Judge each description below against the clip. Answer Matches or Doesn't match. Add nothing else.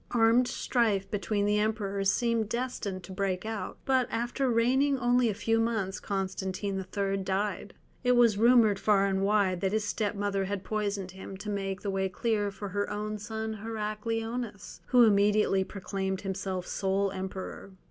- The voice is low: Doesn't match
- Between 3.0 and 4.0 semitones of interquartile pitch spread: Doesn't match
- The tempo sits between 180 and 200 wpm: Doesn't match